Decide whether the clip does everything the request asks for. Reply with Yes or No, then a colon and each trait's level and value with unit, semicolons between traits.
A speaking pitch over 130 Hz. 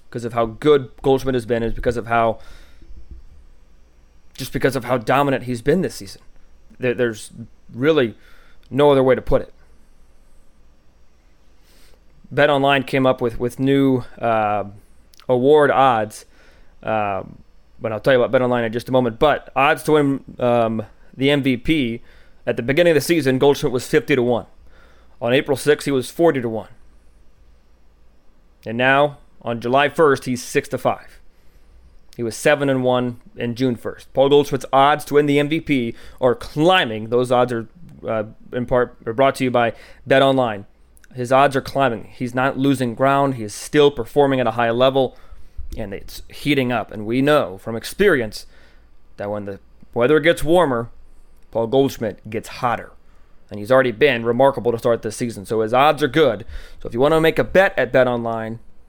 No: low, 120 Hz